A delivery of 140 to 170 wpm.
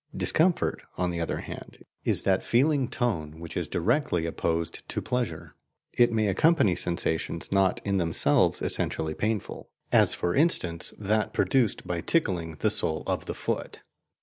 Yes: average, 150 wpm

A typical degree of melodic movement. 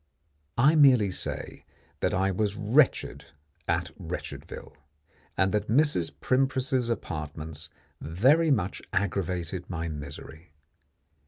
No: wide, 7.4 semitones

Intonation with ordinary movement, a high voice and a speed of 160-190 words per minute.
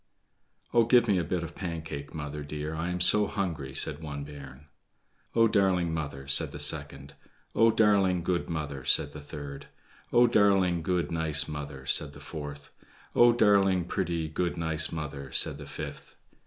No: average, 4.3 semitones; very low, 80 Hz; average, 170 wpm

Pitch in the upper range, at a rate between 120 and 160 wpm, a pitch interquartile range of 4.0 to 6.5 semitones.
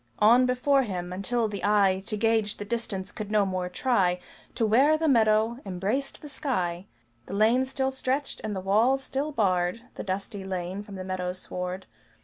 No: high, 210 Hz; average, 180 wpm; average, 4.9 semitones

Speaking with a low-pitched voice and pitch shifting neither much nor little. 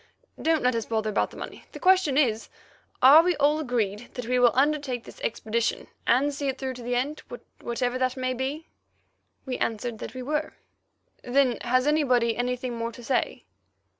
No: very high, 255 Hz; average, 3.0 semitones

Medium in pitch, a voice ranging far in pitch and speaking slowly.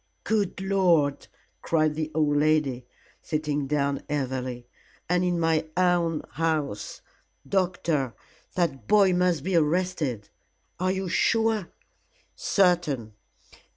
No: medium, 160 Hz; average, 4.1 semitones; slow, 105 wpm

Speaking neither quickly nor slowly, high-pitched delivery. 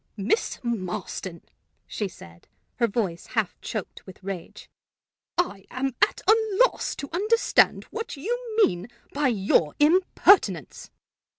No: slow, 120 wpm; high, 235 Hz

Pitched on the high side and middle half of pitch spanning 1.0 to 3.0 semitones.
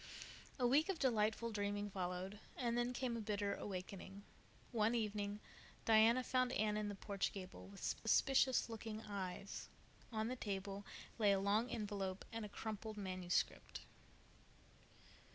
Yes: high, 210 Hz; narrow, 2.5 semitones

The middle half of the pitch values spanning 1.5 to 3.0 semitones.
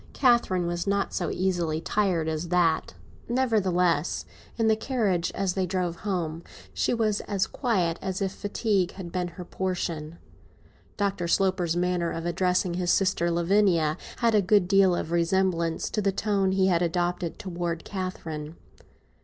Yes: narrow, 2.5 semitones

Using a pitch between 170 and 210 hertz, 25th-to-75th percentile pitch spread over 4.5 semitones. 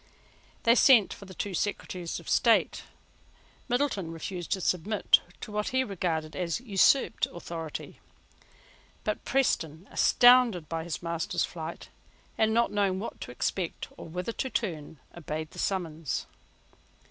Yes: medium, 185 Hz; average, 4.9 semitones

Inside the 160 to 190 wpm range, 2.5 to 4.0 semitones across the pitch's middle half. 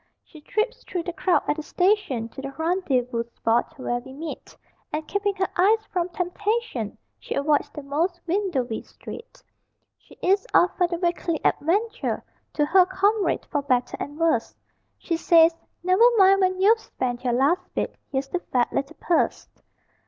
No: average, 165 wpm; wide, 5.4 semitones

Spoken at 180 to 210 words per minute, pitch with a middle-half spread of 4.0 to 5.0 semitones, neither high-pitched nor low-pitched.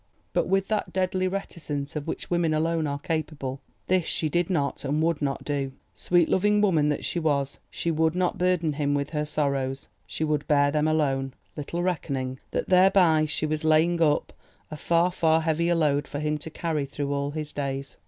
No: average, 190 wpm; average, 3.0 semitones; medium, 155 Hz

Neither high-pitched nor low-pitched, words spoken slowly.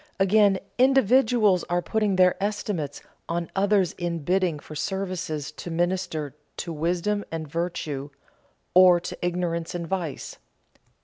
Yes: medium, 180 Hz; slow, 125 wpm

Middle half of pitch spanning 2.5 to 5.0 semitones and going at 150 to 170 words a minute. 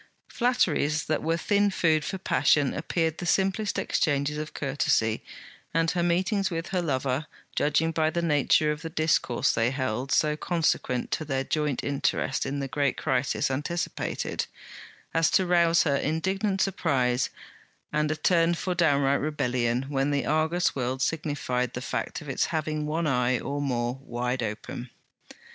Yes: average, 3.7 semitones; average, 155 wpm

